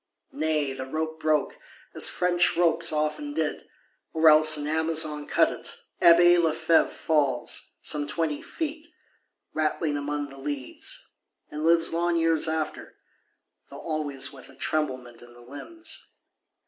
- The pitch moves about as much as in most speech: No, narrow, 2.3 semitones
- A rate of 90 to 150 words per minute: Yes, slow, 135 wpm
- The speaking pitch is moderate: Yes, medium, 155 Hz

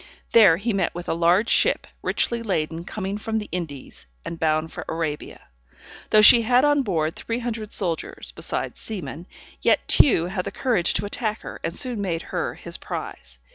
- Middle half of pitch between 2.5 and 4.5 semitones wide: No, average, 5.2 semitones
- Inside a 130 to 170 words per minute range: No, average, 180 wpm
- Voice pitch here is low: No, high, 190 Hz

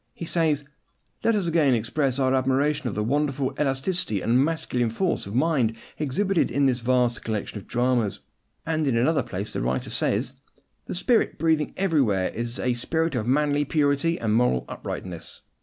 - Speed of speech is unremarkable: Yes, average, 170 wpm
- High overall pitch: No, low, 135 Hz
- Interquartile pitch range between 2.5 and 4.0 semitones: No, average, 4.9 semitones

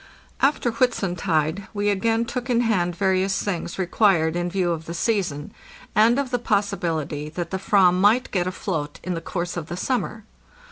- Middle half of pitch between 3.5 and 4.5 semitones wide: Yes, average, 4.1 semitones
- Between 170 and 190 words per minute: Yes, average, 180 wpm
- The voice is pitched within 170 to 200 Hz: Yes, high, 190 Hz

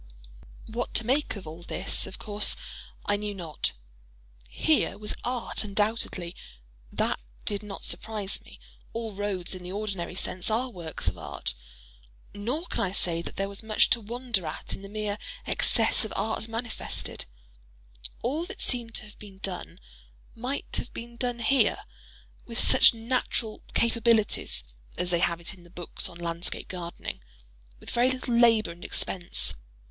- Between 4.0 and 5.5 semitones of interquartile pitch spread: Yes, average, 4.7 semitones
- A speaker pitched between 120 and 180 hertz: No, high, 205 Hz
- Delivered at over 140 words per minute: Yes, average, 155 wpm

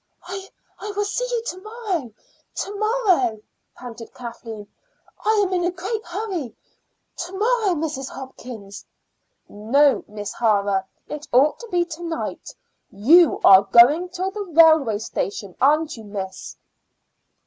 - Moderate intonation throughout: No, wide, 8.9 semitones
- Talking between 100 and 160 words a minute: Yes, slow, 135 wpm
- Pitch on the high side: Yes, very high, 315 Hz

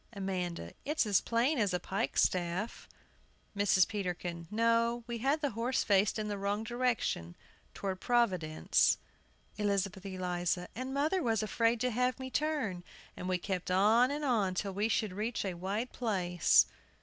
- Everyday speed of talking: Yes, average, 155 wpm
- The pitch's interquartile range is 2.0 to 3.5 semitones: No, average, 4.4 semitones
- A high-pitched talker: Yes, high, 210 Hz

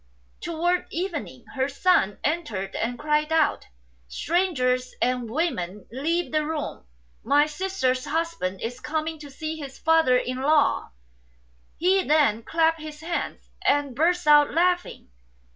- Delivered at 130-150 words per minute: Yes, average, 140 wpm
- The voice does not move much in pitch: No, average, 4.3 semitones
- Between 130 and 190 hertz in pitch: No, very high, 300 Hz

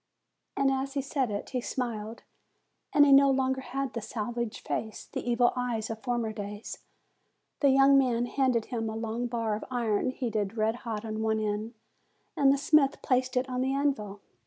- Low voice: No, high, 240 Hz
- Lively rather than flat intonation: No, average, 3.3 semitones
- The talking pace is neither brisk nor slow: Yes, average, 185 wpm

